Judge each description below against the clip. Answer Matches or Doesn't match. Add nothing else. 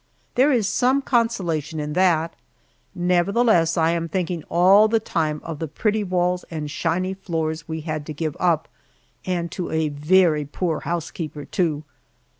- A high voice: Doesn't match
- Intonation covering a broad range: Doesn't match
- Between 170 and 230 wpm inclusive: Doesn't match